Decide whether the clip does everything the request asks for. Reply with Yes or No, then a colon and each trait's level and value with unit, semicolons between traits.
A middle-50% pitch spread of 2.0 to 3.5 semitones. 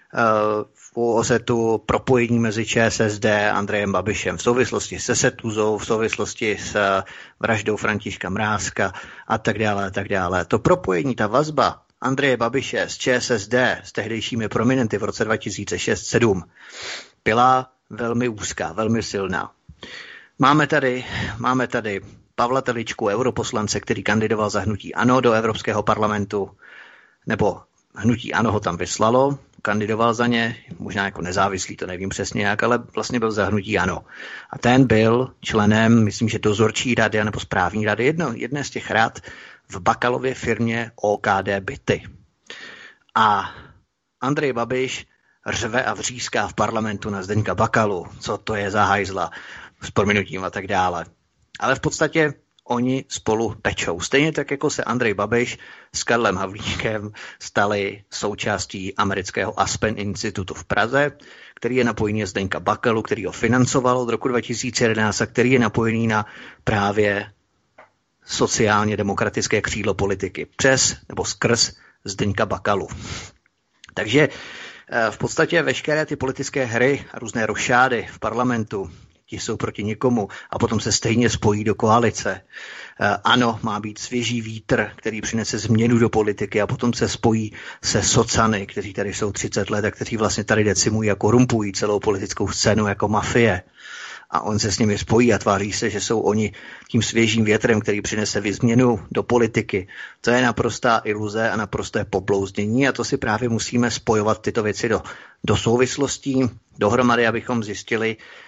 Yes: narrow, 2.6 semitones